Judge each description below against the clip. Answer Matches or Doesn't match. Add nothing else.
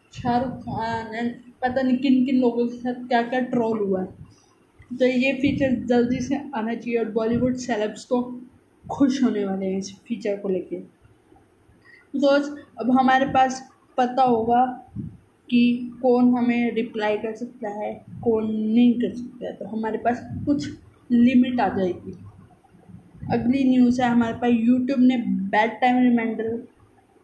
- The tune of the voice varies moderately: Doesn't match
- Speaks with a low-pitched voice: Doesn't match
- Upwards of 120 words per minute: Matches